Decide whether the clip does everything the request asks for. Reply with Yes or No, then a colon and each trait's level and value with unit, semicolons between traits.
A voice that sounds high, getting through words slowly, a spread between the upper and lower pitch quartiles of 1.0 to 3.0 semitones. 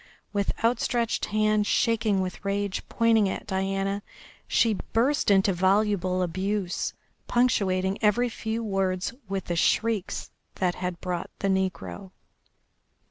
Yes: high, 200 Hz; slow, 120 wpm; narrow, 2.6 semitones